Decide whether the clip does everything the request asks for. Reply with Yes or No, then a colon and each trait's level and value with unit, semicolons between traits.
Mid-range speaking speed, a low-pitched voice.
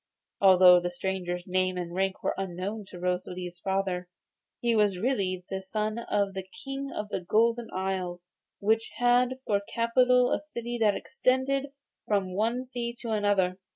No: average, 155 wpm; high, 200 Hz